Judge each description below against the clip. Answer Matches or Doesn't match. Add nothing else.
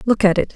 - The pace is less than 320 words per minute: Doesn't match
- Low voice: Doesn't match